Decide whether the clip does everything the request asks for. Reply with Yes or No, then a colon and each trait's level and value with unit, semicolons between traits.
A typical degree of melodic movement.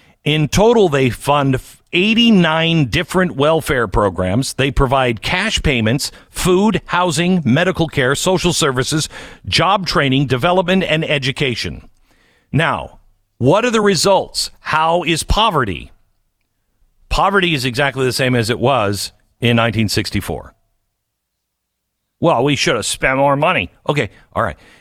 No: wide, 7.0 semitones